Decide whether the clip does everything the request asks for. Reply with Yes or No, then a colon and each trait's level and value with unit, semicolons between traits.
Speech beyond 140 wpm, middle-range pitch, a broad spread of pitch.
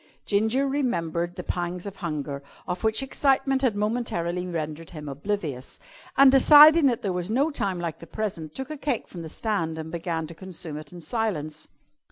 Yes: average, 185 wpm; medium, 180 Hz; wide, 6.7 semitones